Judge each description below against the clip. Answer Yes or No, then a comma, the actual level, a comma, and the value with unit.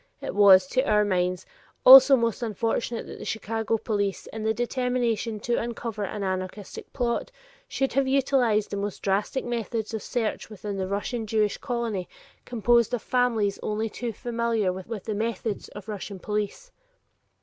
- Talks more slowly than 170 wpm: Yes, average, 160 wpm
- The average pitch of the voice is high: Yes, high, 220 Hz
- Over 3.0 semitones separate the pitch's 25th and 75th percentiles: No, average, 2.7 semitones